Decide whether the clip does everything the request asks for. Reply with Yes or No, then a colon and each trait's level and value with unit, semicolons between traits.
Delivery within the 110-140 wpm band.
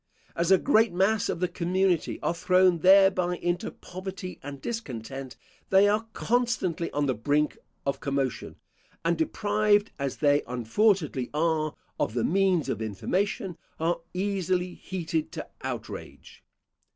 Yes: slow, 135 wpm